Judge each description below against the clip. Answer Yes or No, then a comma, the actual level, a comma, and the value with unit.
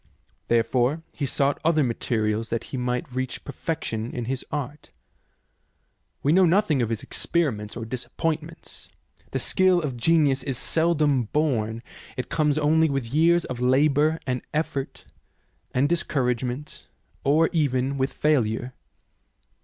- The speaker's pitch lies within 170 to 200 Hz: No, low, 135 Hz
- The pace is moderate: No, slow, 130 wpm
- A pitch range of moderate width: Yes, average, 3.9 semitones